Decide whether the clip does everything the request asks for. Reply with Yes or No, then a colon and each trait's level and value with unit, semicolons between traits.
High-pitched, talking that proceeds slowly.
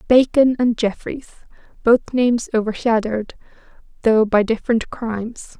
Yes: high, 230 Hz; slow, 105 wpm